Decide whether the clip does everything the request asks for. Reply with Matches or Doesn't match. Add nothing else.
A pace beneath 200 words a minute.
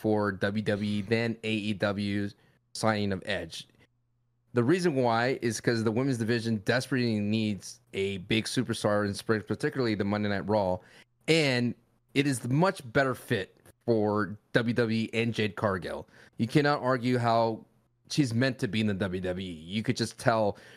Matches